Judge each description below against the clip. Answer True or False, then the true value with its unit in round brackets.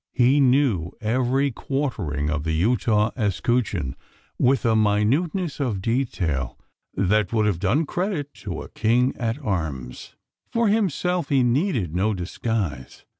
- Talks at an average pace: False (130 wpm)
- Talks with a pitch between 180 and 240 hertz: False (115 Hz)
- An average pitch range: False (6.6 semitones)